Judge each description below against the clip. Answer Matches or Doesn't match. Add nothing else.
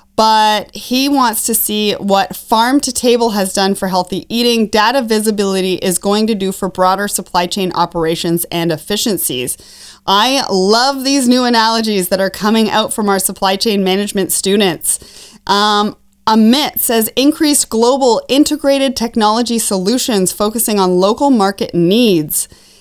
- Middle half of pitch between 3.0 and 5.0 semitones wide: Matches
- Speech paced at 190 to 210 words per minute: Doesn't match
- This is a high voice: Matches